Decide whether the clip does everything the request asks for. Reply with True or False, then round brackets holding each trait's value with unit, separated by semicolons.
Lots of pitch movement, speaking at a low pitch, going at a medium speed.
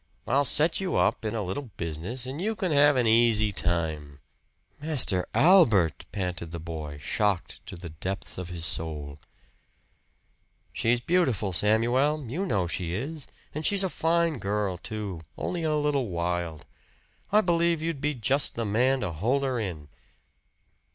True (8.9 semitones; 110 Hz; 160 wpm)